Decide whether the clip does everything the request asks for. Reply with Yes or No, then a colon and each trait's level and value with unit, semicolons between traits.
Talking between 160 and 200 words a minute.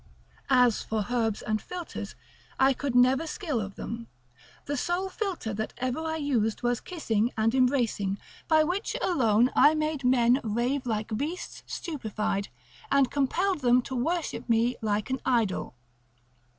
No: average, 150 wpm